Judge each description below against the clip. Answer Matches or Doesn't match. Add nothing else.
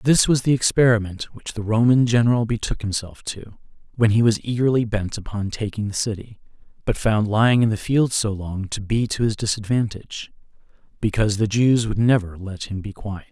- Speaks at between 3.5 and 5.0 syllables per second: Doesn't match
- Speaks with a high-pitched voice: Doesn't match